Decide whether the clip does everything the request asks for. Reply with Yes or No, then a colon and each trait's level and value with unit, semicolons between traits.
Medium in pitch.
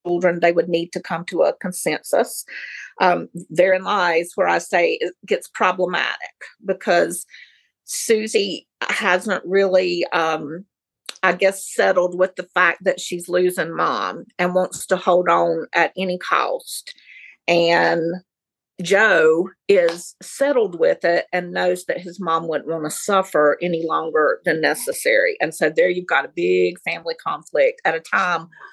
Yes: medium, 180 Hz